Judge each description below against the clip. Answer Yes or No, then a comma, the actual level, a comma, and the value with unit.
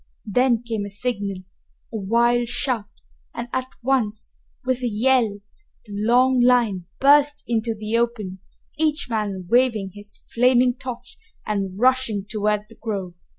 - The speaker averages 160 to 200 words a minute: No, average, 140 wpm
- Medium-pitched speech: No, high, 230 Hz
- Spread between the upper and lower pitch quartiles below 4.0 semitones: Yes, average, 3.3 semitones